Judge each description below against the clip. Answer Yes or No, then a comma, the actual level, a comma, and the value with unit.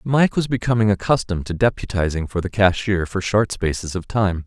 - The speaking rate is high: No, average, 190 wpm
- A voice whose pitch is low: Yes, low, 100 Hz